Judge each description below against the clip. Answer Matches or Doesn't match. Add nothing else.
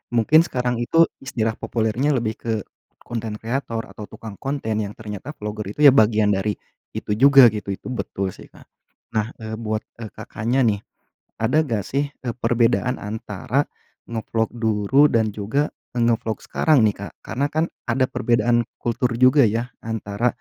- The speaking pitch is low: Matches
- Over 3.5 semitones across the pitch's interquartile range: Doesn't match